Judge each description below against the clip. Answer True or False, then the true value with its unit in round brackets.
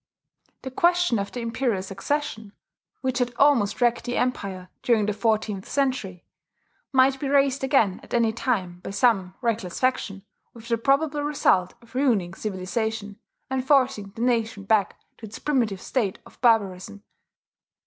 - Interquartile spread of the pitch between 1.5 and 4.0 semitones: False (4.6 semitones)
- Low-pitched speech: False (230 Hz)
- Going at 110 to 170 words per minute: True (150 wpm)